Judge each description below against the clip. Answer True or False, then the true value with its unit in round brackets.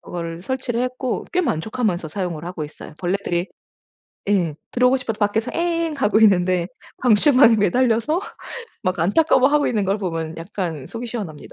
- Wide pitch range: True (6.3 semitones)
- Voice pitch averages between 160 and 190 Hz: False (210 Hz)